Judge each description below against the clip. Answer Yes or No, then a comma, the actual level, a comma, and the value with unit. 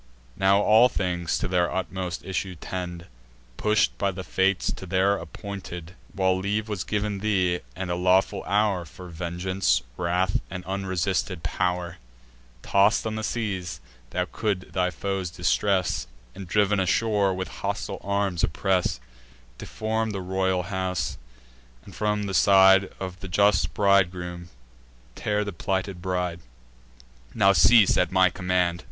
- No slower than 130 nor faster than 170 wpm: Yes, average, 140 wpm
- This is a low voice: Yes, very low, 95 Hz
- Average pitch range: No, narrow, 1.9 semitones